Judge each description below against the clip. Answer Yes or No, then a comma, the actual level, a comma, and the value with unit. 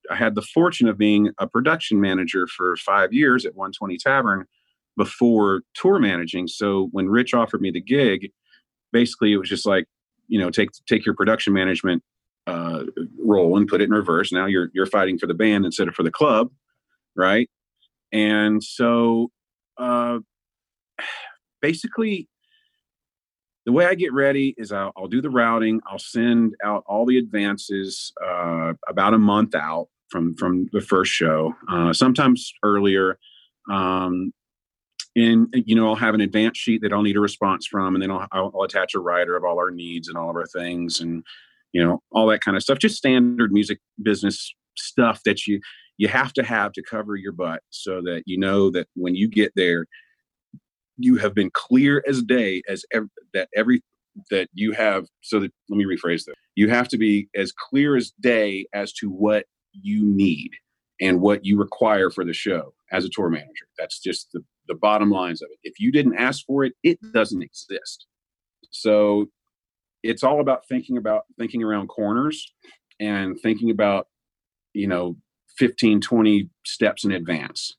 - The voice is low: Yes, low, 105 Hz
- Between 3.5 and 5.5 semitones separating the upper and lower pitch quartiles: Yes, average, 4.0 semitones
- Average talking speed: Yes, average, 180 wpm